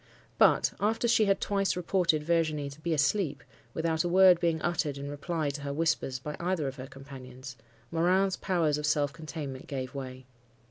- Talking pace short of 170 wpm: No, average, 180 wpm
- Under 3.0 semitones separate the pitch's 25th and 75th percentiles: No, average, 3.7 semitones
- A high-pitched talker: No, medium, 155 Hz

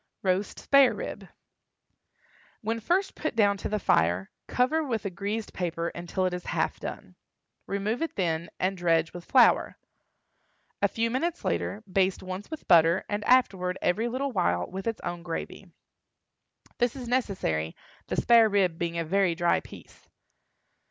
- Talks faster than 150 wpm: Yes, average, 160 wpm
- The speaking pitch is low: No, high, 195 Hz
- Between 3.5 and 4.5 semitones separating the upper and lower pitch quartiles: No, average, 4.9 semitones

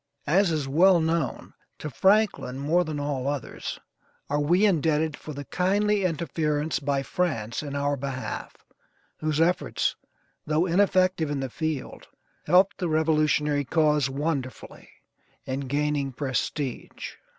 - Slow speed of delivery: Yes, slow, 130 wpm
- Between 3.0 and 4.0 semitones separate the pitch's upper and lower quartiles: Yes, average, 3.3 semitones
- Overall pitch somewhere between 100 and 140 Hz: No, medium, 150 Hz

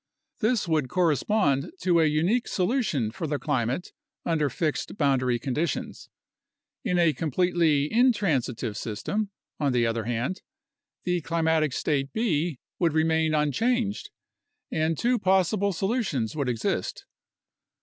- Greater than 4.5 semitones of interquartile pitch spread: Yes, average, 5.3 semitones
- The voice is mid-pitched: Yes, medium, 160 Hz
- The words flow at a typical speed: No, slow, 120 wpm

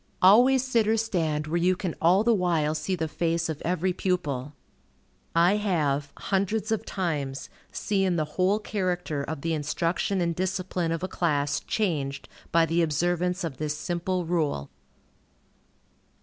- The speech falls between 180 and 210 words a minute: No, average, 150 wpm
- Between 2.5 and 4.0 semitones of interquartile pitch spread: Yes, average, 3.5 semitones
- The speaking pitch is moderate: Yes, medium, 175 Hz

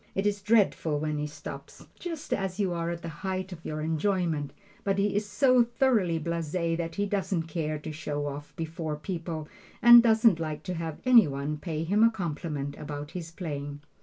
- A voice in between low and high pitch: Yes, medium, 165 Hz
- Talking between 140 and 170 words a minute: No, average, 190 wpm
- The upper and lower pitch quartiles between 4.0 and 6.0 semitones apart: Yes, average, 4.7 semitones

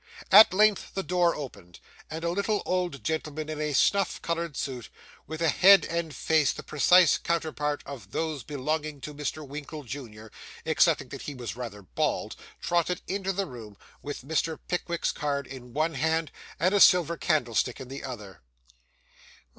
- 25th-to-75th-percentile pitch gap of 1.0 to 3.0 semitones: No, average, 4.1 semitones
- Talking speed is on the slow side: No, average, 165 wpm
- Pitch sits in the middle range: Yes, medium, 155 Hz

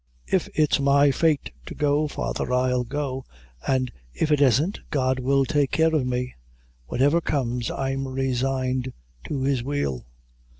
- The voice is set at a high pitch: No, low, 135 Hz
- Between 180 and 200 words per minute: No, average, 145 wpm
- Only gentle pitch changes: Yes, narrow, 2.1 semitones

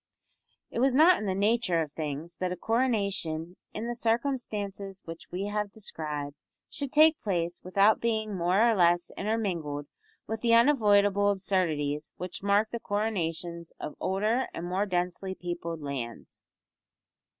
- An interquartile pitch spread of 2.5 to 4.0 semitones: No, average, 4.5 semitones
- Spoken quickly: No, average, 145 wpm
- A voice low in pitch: No, high, 195 Hz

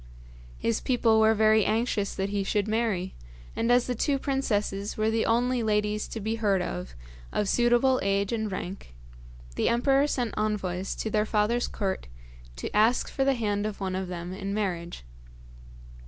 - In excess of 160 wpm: Yes, average, 170 wpm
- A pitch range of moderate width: Yes, average, 3.1 semitones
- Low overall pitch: No, high, 215 Hz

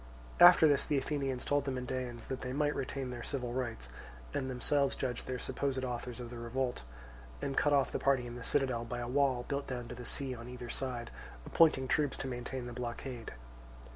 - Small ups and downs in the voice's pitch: Yes, narrow, 2.1 semitones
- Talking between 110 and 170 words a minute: No, fast, 205 wpm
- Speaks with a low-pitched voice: Yes, low, 130 Hz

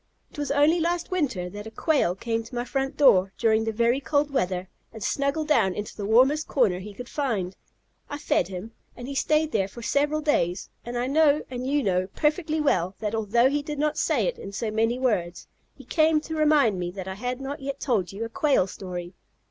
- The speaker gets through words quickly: Yes, fast, 220 wpm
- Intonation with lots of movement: Yes, wide, 6.4 semitones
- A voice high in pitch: Yes, high, 245 Hz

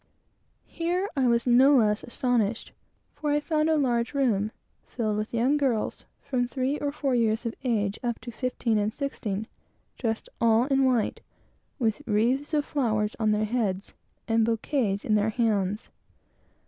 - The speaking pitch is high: Yes, high, 235 Hz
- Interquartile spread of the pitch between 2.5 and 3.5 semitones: No, average, 3.9 semitones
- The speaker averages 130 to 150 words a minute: No, average, 160 wpm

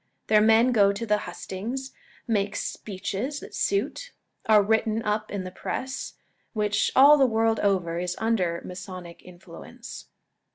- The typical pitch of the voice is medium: No, high, 210 Hz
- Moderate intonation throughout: Yes, average, 3.4 semitones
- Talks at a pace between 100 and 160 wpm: Yes, average, 140 wpm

